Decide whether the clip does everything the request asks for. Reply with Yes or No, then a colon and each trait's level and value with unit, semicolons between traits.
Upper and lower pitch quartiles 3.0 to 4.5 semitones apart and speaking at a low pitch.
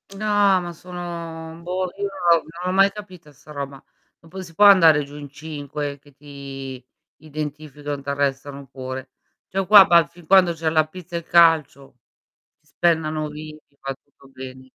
No: average, 3.6 semitones; medium, 155 Hz